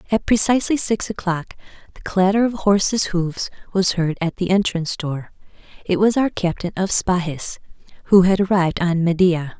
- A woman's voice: Yes, female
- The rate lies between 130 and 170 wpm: Yes, average, 165 wpm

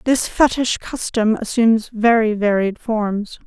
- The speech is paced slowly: Yes, slow, 120 wpm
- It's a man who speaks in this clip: No, female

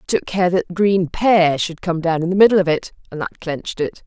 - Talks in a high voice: No, medium, 175 Hz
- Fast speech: Yes, fast, 265 wpm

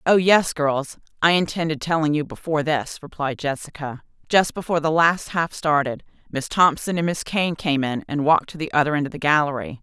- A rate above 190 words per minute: Yes, average, 200 wpm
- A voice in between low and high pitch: Yes, medium, 155 Hz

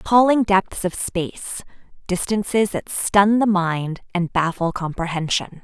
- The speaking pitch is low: No, high, 190 Hz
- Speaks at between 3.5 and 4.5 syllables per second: Yes, 4.2 syllables/s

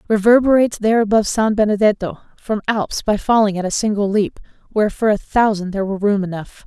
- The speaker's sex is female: Yes, female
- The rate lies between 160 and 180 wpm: No, average, 190 wpm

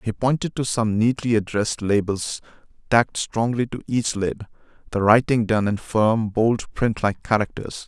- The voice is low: Yes, low, 110 Hz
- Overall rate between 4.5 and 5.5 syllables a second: Yes, 4.6 syllables/s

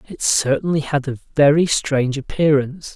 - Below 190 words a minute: Yes, average, 140 wpm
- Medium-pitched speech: Yes, medium, 145 Hz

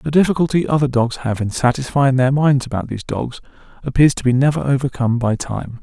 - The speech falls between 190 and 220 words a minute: Yes, average, 195 wpm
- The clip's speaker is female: No, male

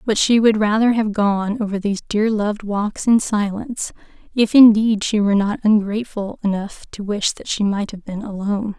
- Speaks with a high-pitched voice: Yes, high, 210 Hz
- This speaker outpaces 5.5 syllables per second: No, 5.2 syllables/s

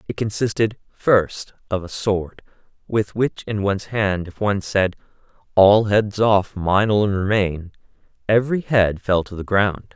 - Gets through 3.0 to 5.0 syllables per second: Yes, 4.5 syllables/s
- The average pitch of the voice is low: Yes, low, 100 Hz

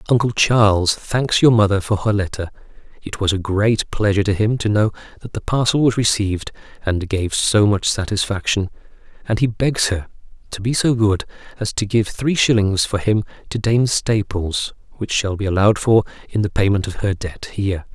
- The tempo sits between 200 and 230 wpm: No, average, 190 wpm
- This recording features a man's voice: Yes, male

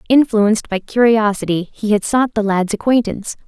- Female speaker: Yes, female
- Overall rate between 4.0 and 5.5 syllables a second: Yes, 5.3 syllables/s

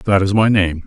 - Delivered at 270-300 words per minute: Yes, fast, 280 wpm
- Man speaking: Yes, male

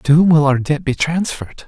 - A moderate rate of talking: No, fast, 250 wpm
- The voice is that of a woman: No, male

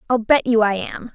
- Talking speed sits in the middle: No, fast, 260 wpm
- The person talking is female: Yes, female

